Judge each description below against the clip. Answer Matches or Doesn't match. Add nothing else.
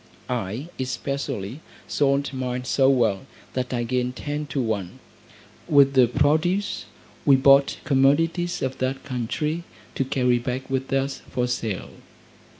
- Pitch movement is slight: Matches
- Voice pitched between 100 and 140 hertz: Matches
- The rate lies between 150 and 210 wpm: Doesn't match